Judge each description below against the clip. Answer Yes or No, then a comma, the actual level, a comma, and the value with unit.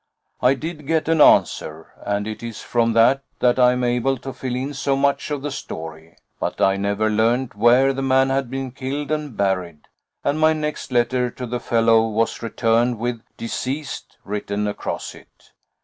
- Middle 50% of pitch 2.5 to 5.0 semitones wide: Yes, average, 3.4 semitones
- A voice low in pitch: Yes, low, 125 Hz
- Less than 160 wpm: No, average, 180 wpm